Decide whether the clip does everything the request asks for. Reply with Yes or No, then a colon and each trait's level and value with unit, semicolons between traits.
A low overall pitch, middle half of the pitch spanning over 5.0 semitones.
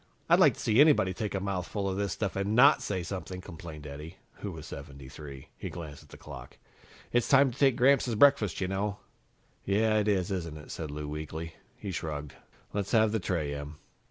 Yes: very low, 95 Hz; wide, 5.6 semitones